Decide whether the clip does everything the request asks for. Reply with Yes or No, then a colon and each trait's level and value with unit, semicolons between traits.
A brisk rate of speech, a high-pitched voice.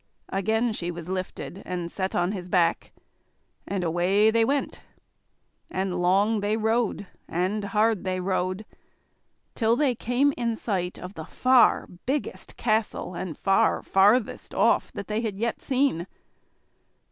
No: slow, 135 wpm; high, 200 Hz